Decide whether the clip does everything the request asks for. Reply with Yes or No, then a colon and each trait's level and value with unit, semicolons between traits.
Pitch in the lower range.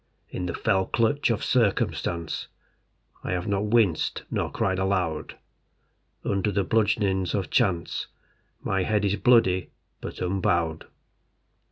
Yes: very low, 95 Hz